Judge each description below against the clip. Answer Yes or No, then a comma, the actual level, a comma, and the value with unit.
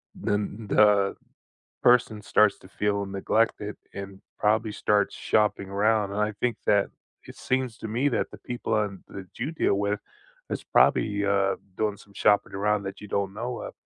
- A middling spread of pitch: No, narrow, 1.6 semitones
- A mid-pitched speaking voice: No, low, 105 Hz